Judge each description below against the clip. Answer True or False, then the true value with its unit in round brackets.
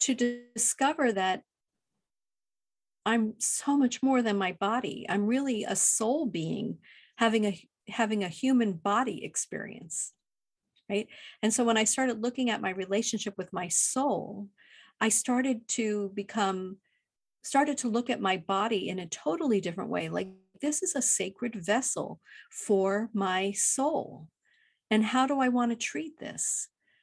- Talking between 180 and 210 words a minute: False (150 wpm)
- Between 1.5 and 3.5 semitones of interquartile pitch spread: False (4.2 semitones)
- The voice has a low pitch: False (225 Hz)